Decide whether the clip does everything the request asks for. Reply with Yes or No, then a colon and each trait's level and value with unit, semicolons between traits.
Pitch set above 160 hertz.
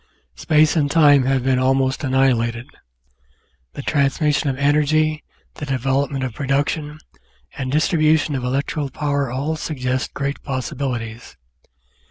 No: medium, 140 Hz